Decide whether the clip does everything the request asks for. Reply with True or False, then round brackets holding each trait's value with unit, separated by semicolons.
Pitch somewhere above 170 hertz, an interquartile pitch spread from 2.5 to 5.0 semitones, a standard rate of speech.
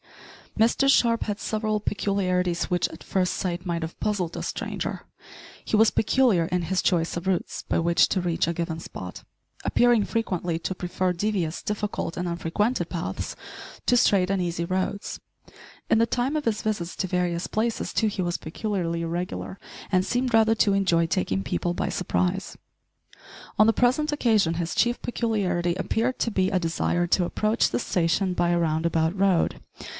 True (185 Hz; 3.9 semitones; 175 wpm)